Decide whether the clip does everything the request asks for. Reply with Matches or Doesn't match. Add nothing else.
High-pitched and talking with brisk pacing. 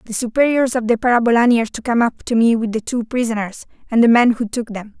Matches